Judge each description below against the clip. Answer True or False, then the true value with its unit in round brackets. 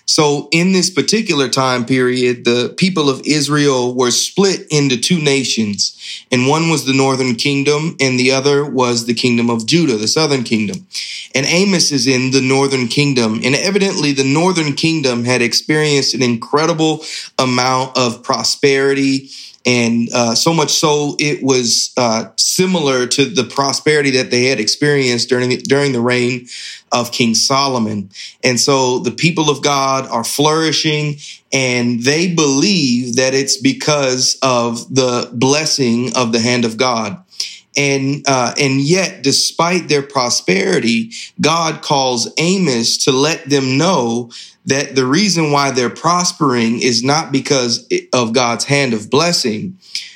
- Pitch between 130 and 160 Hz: True (135 Hz)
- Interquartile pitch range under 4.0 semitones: True (3.2 semitones)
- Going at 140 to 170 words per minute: True (150 wpm)